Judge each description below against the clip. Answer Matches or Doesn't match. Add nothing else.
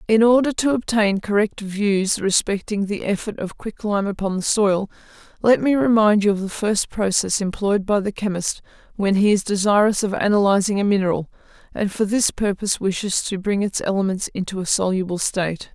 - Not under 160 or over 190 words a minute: Matches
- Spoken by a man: Doesn't match